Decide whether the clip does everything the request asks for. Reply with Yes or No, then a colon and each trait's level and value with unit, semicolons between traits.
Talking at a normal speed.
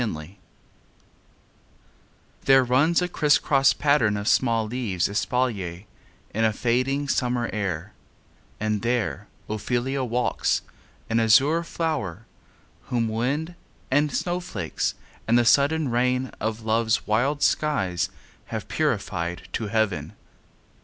No: slow, 110 wpm